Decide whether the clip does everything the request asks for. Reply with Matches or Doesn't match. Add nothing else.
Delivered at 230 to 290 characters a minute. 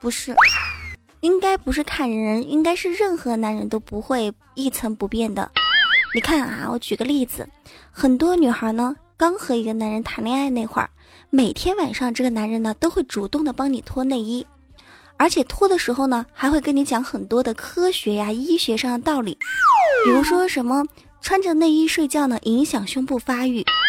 Matches